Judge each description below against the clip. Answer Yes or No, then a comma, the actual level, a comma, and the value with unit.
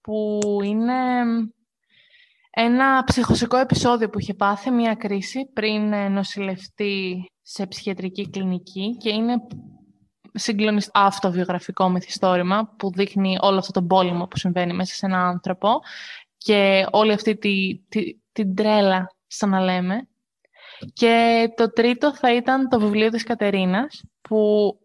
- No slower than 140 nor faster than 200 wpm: No, average, 130 wpm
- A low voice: No, high, 205 Hz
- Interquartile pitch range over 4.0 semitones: No, average, 3.2 semitones